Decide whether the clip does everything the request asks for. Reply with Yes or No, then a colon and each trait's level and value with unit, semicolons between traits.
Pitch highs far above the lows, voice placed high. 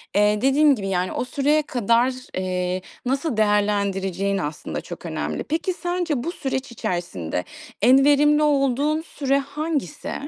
Yes: wide, 6.9 semitones; very high, 260 Hz